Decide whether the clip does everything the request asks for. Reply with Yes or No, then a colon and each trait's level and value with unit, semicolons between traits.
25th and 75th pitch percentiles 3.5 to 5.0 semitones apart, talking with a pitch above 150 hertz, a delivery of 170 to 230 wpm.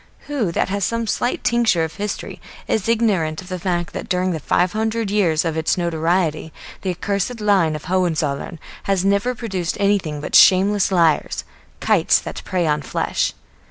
Yes: average, 4.0 semitones; medium, 185 Hz; average, 175 wpm